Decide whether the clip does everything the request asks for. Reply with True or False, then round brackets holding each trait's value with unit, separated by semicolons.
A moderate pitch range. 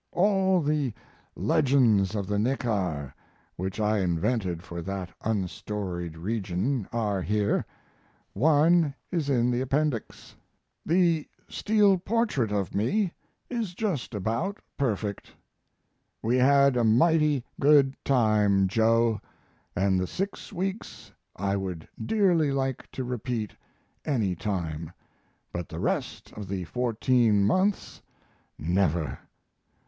False (6.8 semitones)